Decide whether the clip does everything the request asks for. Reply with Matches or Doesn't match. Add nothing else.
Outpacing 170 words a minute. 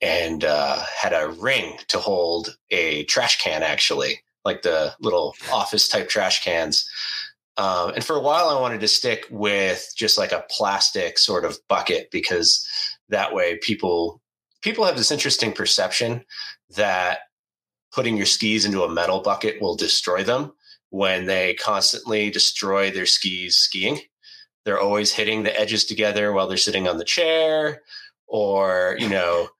Doesn't match